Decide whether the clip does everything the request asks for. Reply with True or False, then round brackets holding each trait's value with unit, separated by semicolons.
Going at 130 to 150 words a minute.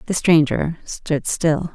True (135 wpm)